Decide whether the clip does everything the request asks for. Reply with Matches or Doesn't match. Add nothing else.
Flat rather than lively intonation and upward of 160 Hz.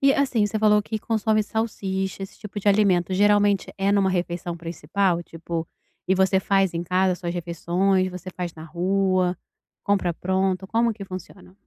Matches